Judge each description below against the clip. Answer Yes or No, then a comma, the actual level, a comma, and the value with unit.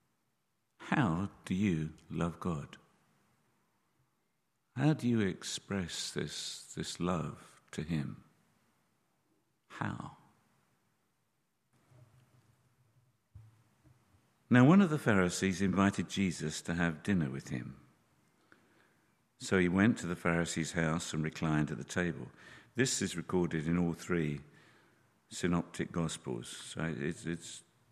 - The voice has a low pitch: Yes, very low, 95 Hz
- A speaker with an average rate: No, slow, 105 wpm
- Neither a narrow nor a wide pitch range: No, wide, 6.0 semitones